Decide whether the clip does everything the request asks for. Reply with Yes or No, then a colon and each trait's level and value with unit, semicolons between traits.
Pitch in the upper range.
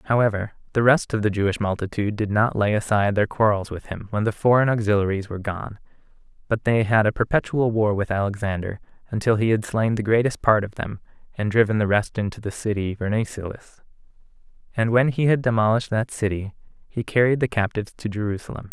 No: low, 110 Hz